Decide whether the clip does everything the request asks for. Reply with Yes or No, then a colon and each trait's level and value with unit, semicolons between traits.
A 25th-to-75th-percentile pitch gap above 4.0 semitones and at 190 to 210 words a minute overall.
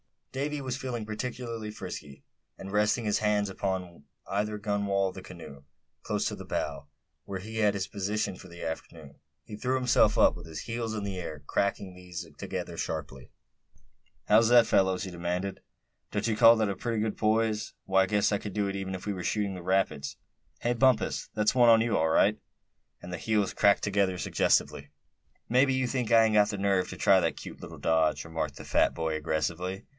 No: average, 3.4 semitones; fast, 205 wpm